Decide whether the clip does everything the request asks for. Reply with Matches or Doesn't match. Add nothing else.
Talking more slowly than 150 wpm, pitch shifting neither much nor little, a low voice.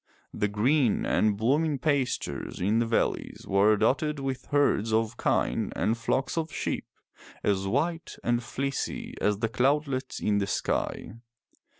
Matches